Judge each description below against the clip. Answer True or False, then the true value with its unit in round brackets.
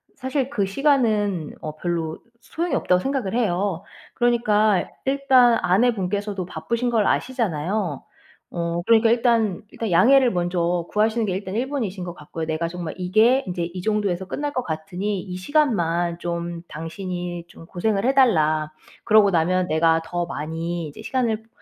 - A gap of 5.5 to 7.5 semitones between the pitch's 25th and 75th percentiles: False (5.1 semitones)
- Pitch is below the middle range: False (190 Hz)